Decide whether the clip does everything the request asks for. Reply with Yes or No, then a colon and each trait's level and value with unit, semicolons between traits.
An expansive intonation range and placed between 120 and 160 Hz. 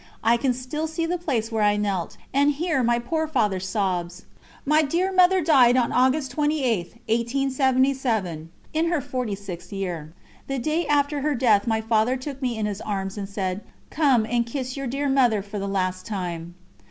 No: wide, 5.8 semitones; high, 240 Hz